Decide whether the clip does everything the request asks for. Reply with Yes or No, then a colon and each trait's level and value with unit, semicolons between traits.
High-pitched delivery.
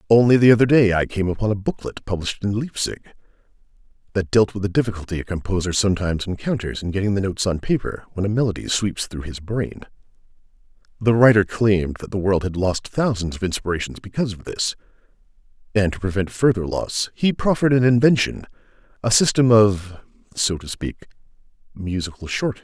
No: low, 100 Hz